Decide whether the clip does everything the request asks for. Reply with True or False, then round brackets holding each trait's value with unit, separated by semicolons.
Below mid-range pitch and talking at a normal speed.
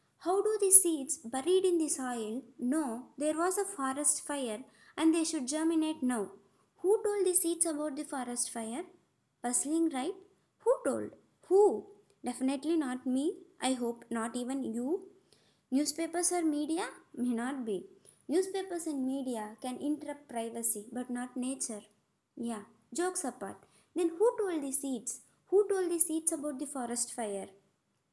False (290 Hz; 150 wpm)